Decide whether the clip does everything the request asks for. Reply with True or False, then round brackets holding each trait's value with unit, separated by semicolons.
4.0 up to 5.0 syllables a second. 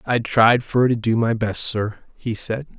True (4.1 syllables/s)